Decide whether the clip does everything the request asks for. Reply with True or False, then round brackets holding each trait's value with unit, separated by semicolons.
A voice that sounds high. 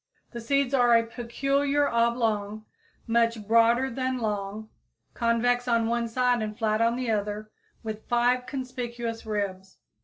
True (235 Hz)